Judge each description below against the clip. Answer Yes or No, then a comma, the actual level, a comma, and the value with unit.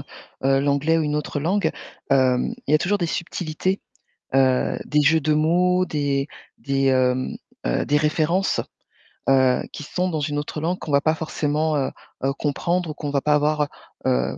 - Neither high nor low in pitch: Yes, medium, 150 Hz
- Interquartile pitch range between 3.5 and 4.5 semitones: No, average, 2.7 semitones